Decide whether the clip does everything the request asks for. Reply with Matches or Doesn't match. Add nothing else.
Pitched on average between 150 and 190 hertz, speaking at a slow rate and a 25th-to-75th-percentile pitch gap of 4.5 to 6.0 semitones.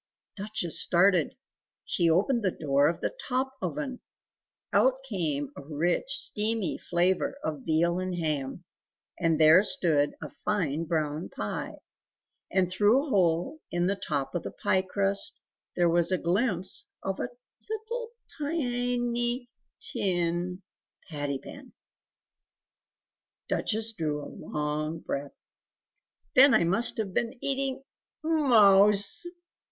Matches